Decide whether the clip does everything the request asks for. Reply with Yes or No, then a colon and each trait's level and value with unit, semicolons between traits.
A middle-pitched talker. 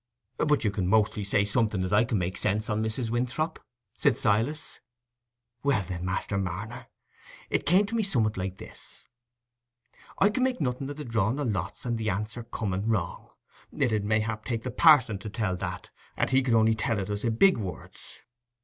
No: low, 110 Hz